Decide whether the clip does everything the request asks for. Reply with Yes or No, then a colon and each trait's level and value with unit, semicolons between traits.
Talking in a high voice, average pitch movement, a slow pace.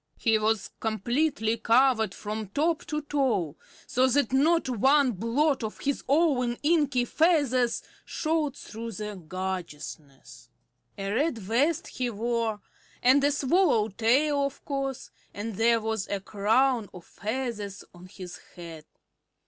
Yes: high, 235 Hz; average, 5.0 semitones; slow, 130 wpm